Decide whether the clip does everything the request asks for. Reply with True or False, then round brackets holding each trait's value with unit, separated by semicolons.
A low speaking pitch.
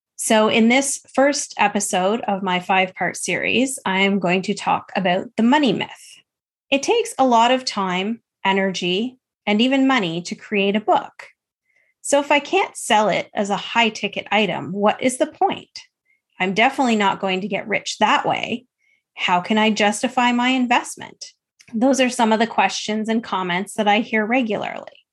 False (220 Hz)